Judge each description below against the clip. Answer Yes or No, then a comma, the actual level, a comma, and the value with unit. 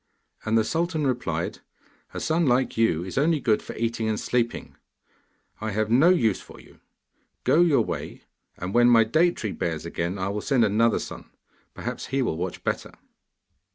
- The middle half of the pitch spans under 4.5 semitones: No, average, 5.1 semitones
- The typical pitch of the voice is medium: No, low, 115 Hz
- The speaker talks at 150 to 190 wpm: Yes, average, 180 wpm